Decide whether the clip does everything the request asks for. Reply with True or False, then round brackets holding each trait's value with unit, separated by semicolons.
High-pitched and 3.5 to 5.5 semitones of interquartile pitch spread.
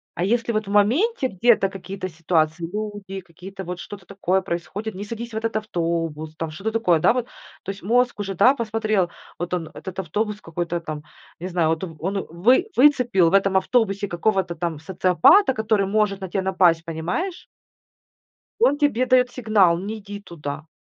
True (195 Hz; 4.2 semitones)